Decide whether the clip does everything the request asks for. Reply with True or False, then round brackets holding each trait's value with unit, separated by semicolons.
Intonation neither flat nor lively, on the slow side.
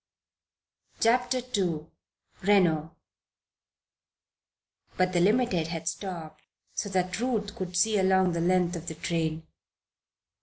True (3.5 semitones; 110 wpm)